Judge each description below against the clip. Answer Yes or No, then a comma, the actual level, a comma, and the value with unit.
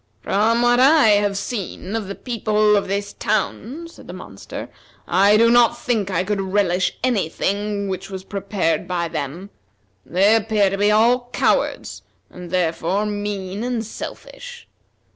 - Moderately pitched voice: No, high, 205 Hz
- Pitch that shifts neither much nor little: Yes, average, 3.2 semitones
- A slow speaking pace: No, average, 155 wpm